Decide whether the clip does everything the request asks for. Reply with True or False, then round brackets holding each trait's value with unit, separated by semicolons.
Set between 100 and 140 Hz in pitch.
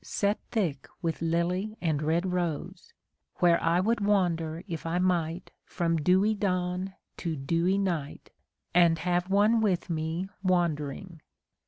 False (175 Hz)